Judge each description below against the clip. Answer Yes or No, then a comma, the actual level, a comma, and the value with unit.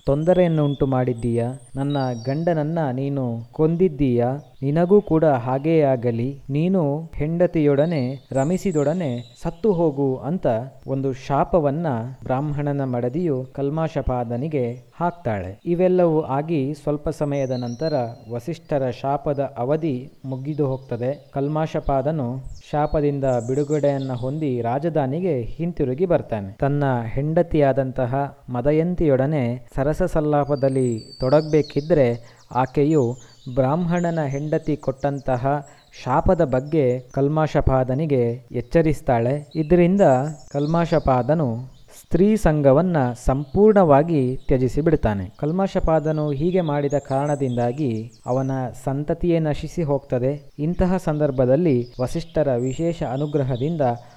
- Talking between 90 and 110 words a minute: No, average, 80 wpm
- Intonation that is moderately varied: Yes, average, 3.3 semitones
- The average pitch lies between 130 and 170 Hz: Yes, medium, 140 Hz